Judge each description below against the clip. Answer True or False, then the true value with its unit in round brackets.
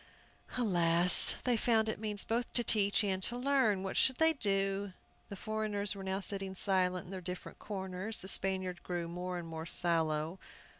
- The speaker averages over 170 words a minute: True (180 wpm)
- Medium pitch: False (195 Hz)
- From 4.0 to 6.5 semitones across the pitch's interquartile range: False (3.1 semitones)